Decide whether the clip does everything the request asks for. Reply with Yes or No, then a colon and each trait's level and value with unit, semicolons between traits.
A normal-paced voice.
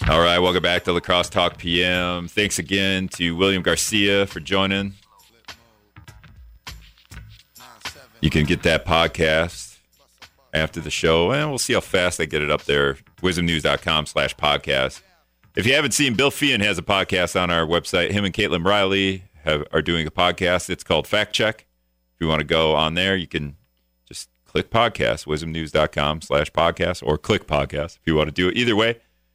Yes: average, 180 wpm